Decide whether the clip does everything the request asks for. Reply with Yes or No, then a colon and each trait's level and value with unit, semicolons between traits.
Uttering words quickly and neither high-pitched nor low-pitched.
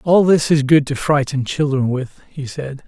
Yes: fast, 210 wpm; medium, 145 Hz